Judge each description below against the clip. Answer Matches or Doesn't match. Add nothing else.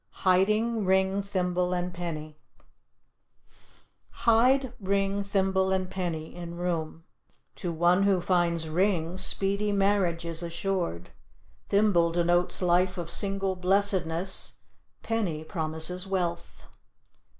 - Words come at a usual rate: Doesn't match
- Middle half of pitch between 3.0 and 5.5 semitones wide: Doesn't match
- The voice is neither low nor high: Matches